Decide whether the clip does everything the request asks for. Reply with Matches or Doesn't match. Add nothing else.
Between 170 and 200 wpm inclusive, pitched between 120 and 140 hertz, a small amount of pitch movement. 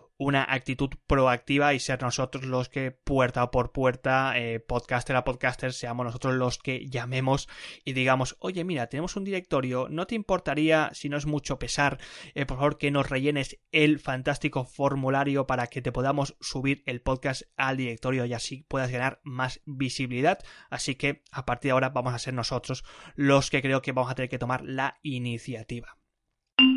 Matches